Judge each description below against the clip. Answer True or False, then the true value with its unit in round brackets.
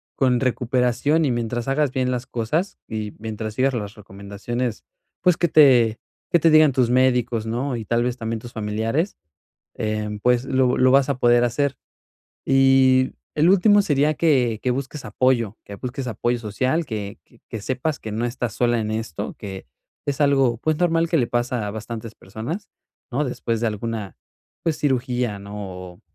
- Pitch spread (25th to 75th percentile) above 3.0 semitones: True (3.4 semitones)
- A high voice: False (125 Hz)